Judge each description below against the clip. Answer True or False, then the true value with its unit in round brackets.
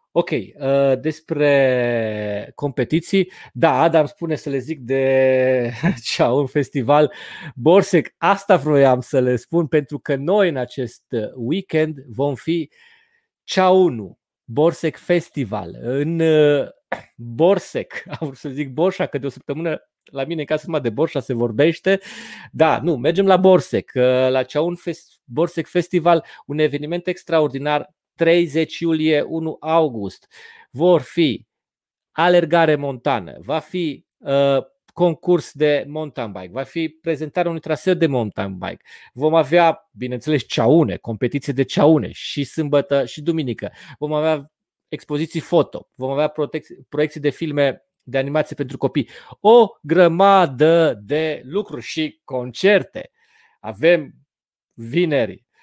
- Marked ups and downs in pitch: False (3.8 semitones)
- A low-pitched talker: False (155 Hz)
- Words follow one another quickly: False (125 wpm)